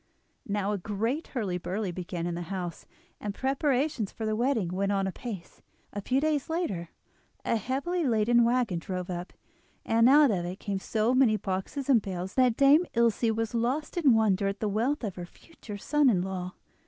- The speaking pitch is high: Yes, high, 215 Hz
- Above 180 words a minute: Yes, average, 190 wpm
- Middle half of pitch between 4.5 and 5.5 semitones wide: Yes, average, 5.2 semitones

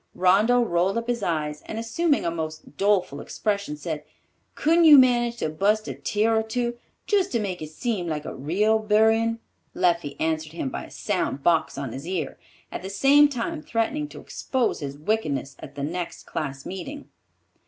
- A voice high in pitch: Yes, high, 200 Hz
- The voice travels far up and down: Yes, wide, 6.9 semitones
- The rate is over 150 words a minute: Yes, average, 185 wpm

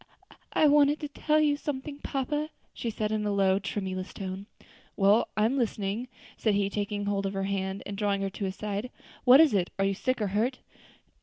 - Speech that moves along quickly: Yes, fast, 210 wpm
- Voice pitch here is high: Yes, high, 210 Hz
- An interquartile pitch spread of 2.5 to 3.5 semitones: No, average, 4.9 semitones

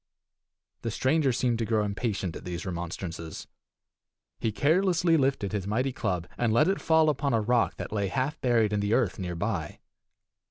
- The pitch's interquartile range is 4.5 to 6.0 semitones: Yes, wide, 5.6 semitones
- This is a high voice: No, low, 115 Hz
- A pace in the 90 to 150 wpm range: No, average, 175 wpm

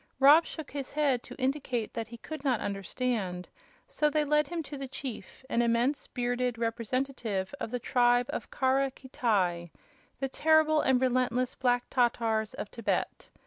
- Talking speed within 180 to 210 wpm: No, average, 160 wpm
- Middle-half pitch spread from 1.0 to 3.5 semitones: Yes, average, 2.9 semitones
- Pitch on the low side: No, very high, 250 Hz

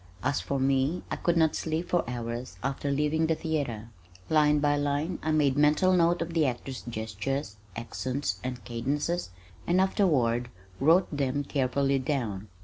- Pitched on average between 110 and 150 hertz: Yes, medium, 140 Hz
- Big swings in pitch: No, average, 3.9 semitones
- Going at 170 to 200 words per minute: No, average, 155 wpm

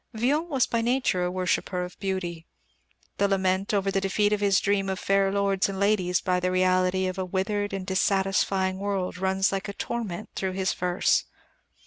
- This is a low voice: No, high, 195 Hz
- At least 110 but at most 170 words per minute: No, average, 185 wpm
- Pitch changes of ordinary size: No, narrow, 1.4 semitones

